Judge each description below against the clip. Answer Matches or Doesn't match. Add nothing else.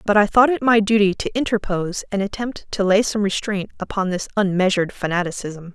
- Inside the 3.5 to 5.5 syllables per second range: Doesn't match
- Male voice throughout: Doesn't match